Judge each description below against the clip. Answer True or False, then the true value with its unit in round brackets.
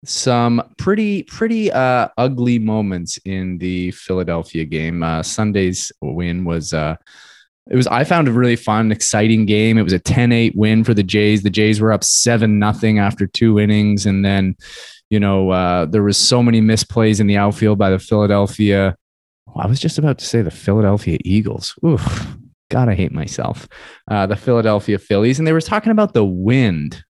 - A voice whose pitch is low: True (105 Hz)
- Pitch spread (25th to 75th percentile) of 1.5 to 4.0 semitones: True (3.7 semitones)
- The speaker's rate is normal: True (185 wpm)